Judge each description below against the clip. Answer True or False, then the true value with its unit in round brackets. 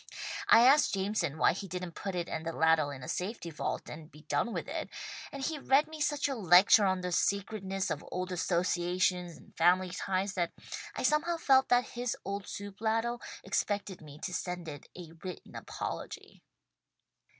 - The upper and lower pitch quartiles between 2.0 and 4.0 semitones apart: False (4.6 semitones)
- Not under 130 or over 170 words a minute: False (185 wpm)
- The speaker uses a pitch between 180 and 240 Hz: True (185 Hz)